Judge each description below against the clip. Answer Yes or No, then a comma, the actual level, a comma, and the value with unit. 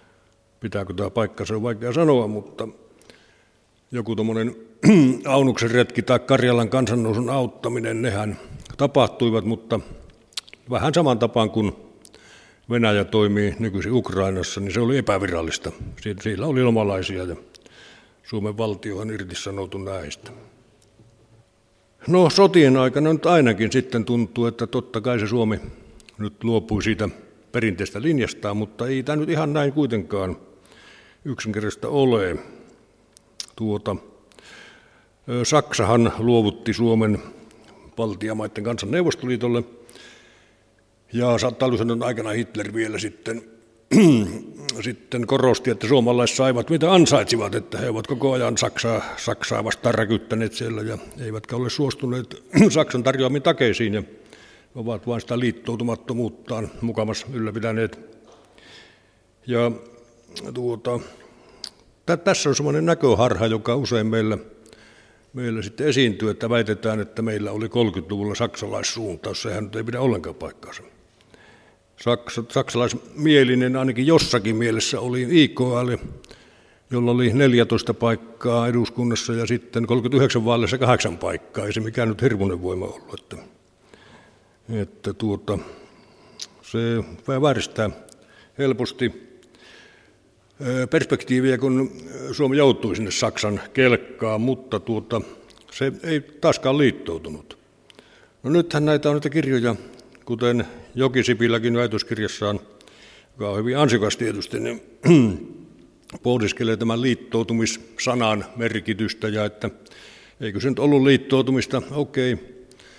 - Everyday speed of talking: Yes, average, 110 wpm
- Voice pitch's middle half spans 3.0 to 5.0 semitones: No, narrow, 2.6 semitones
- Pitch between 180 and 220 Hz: No, low, 115 Hz